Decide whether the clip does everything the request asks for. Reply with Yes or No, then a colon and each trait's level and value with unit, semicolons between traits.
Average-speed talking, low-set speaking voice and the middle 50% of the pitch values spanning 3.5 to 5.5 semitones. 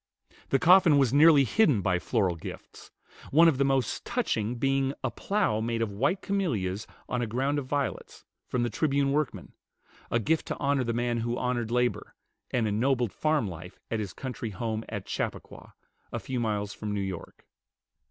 Yes: average, 180 wpm; low, 125 Hz; average, 4.3 semitones